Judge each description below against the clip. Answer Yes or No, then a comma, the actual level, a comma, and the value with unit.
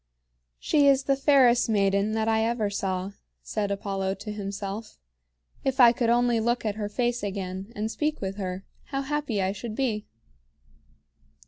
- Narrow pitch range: No, average, 3.5 semitones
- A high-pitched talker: Yes, high, 215 Hz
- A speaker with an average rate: Yes, average, 160 wpm